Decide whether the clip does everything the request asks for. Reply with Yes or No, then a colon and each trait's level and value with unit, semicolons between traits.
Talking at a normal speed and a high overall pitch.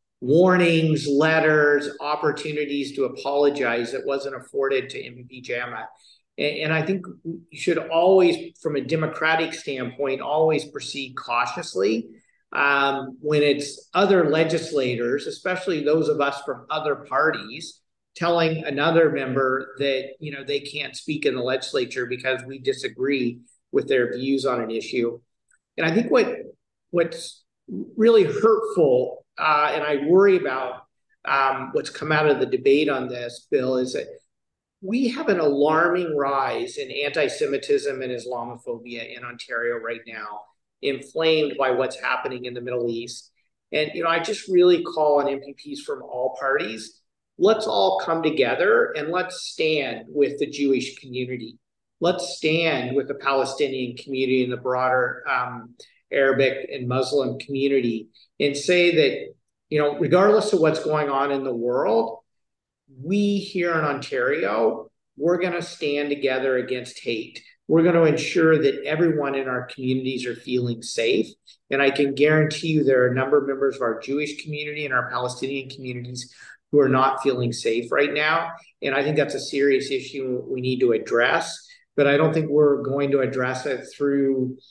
No: average, 155 wpm; medium, 140 Hz